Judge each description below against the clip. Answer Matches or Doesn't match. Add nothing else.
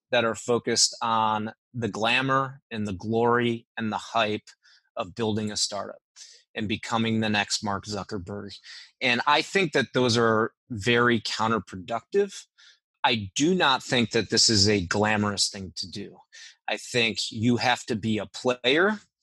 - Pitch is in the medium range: Doesn't match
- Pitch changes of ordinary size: Doesn't match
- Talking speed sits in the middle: Matches